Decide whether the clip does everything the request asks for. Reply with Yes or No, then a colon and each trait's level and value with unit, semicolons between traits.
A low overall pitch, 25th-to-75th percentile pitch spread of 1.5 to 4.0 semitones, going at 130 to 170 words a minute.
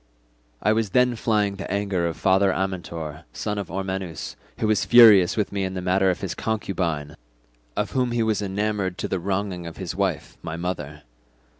No: very low, 95 Hz; average, 2.7 semitones; average, 185 wpm